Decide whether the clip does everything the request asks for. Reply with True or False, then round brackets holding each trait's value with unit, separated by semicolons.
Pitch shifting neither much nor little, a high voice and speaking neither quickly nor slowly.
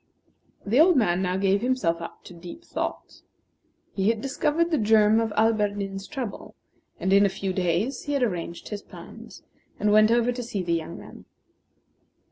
True (4.3 semitones; 210 Hz; 175 wpm)